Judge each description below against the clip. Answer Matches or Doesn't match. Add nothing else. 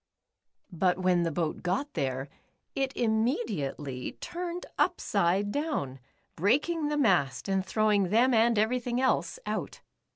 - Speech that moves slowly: Matches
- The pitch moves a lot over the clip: Matches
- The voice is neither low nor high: Doesn't match